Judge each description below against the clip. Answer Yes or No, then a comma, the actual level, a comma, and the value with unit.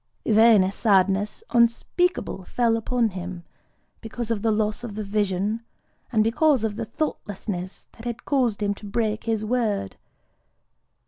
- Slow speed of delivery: No, average, 145 wpm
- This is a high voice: Yes, high, 220 Hz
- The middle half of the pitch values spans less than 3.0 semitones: Yes, narrow, 2.5 semitones